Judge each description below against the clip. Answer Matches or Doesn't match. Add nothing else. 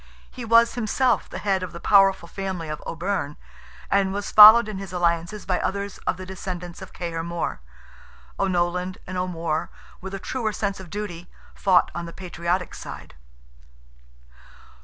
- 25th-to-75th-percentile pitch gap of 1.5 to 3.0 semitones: Matches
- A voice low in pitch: Doesn't match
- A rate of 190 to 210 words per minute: Doesn't match